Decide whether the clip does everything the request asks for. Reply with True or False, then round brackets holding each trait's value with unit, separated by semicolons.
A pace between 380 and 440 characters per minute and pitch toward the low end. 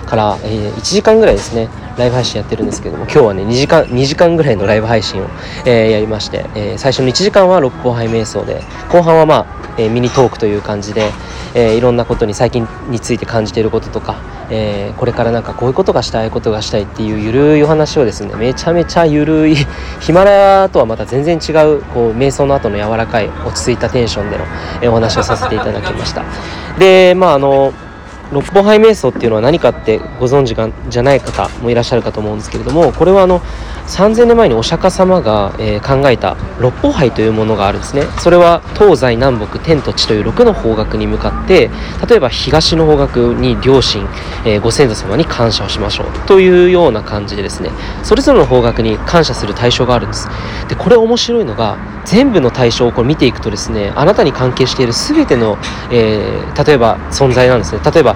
True (430 characters per minute; 120 Hz)